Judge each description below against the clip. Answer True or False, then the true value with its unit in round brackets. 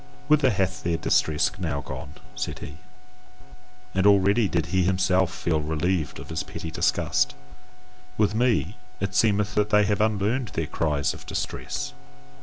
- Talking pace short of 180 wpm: True (150 wpm)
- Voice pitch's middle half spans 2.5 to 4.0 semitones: False (4.7 semitones)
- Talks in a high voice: False (95 Hz)